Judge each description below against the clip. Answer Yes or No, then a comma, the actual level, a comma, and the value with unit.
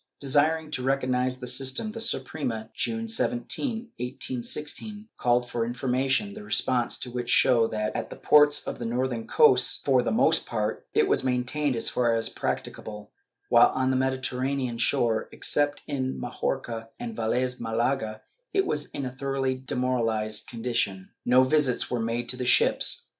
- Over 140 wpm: Yes, average, 160 wpm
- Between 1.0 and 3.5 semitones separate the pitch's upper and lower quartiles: Yes, average, 2.9 semitones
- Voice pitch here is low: Yes, low, 130 Hz